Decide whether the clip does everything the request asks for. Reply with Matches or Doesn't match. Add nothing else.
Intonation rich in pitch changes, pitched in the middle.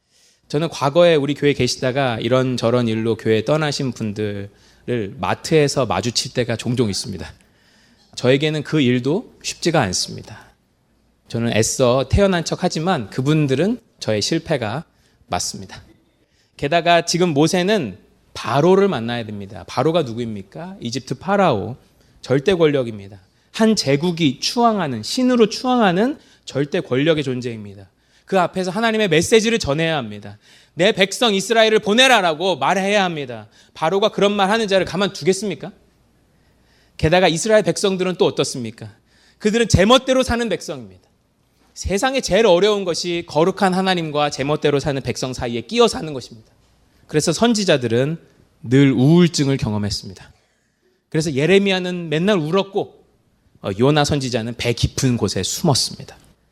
Matches